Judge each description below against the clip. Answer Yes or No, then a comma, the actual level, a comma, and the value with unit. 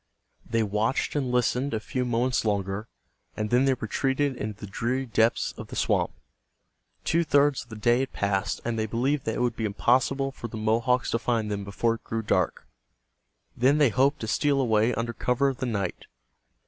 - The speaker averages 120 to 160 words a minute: No, average, 200 wpm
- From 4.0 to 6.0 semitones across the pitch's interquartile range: No, average, 3.3 semitones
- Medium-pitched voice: No, low, 120 Hz